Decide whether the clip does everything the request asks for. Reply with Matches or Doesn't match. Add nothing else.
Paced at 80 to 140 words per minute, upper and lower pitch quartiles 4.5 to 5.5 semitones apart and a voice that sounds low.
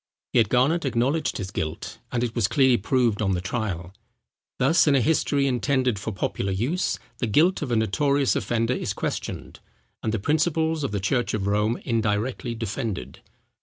Doesn't match